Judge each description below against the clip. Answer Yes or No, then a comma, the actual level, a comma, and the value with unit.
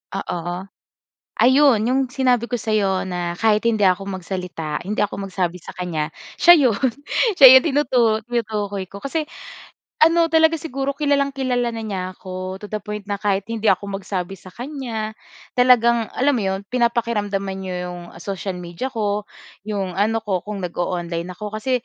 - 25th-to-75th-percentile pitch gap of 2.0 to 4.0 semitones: No, average, 4.7 semitones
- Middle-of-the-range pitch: No, high, 210 Hz